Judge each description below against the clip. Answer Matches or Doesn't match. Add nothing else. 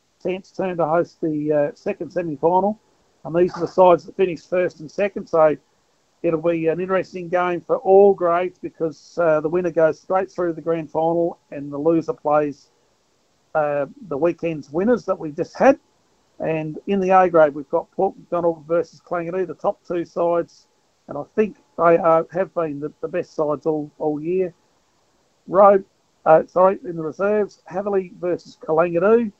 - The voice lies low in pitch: Doesn't match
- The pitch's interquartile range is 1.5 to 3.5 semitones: Matches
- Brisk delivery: Doesn't match